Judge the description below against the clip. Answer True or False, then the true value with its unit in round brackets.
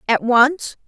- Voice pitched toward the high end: True (250 Hz)